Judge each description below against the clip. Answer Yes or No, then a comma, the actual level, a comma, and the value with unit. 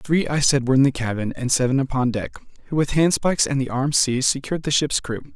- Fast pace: Yes, fast, 245 wpm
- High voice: No, low, 135 Hz